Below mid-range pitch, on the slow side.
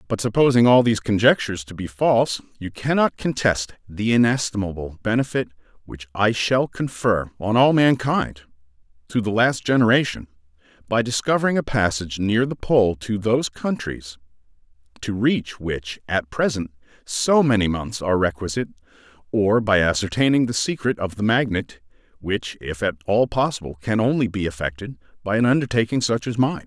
No: low, 110 Hz; average, 155 wpm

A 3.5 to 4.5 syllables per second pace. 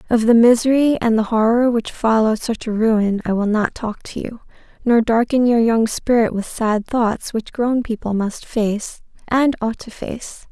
Yes: 4.3 syllables/s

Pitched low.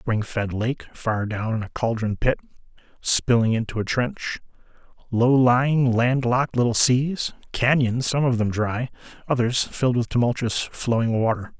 Yes: low, 120 Hz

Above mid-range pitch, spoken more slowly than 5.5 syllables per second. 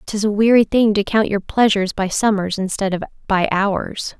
Yes: high, 205 Hz; 5.0 syllables/s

